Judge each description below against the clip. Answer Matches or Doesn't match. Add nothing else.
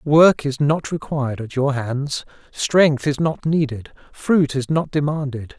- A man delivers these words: Matches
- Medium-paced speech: Matches